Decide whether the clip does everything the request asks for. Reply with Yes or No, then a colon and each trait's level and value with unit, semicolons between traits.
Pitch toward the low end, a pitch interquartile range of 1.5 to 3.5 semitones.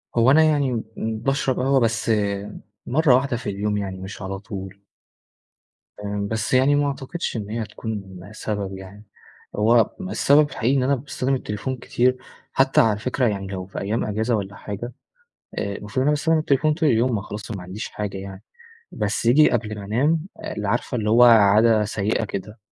No: low, 110 Hz; average, 4.3 semitones